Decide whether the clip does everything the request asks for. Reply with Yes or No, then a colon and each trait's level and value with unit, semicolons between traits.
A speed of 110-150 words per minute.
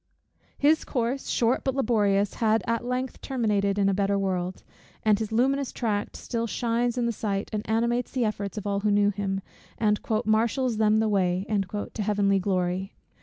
No: average, 175 wpm